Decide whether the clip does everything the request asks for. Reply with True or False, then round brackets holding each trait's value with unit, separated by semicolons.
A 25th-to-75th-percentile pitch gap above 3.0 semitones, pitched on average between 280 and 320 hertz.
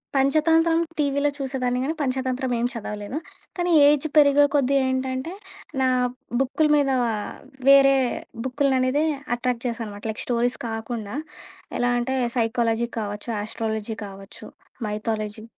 False (3.6 semitones; 255 Hz)